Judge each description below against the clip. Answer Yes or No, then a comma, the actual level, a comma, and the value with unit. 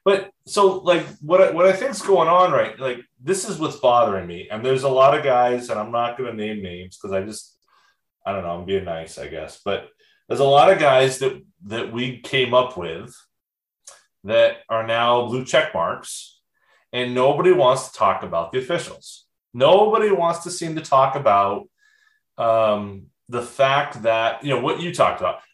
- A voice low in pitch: Yes, low, 130 Hz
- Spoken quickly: No, average, 195 wpm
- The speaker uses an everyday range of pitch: No, wide, 8.2 semitones